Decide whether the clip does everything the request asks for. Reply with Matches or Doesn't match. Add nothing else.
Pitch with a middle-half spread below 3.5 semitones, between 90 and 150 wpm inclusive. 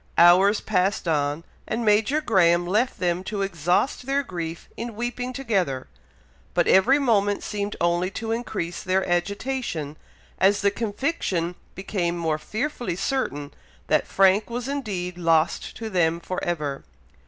Doesn't match